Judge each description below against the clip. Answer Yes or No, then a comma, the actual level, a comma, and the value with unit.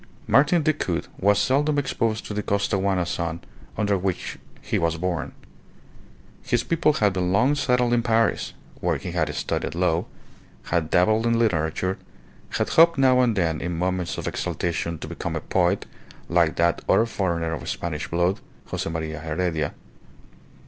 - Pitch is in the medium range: No, very low, 95 Hz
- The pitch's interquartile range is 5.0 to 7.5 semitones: Yes, wide, 5.6 semitones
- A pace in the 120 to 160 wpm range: Yes, average, 155 wpm